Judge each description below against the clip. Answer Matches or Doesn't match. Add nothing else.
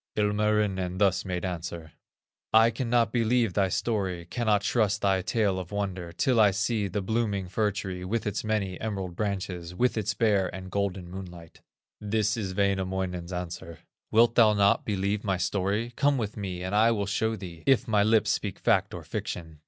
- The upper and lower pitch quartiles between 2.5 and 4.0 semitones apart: Matches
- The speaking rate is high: Doesn't match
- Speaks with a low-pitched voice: Matches